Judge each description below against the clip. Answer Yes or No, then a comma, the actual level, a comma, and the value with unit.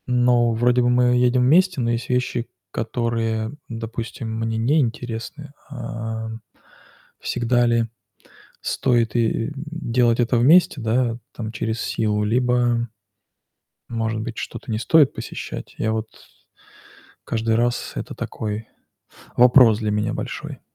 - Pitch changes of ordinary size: No, narrow, 1.7 semitones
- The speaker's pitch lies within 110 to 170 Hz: Yes, low, 120 Hz